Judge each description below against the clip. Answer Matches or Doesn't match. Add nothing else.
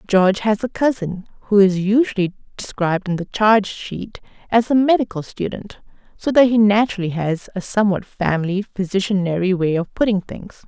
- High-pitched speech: Matches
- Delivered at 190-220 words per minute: Doesn't match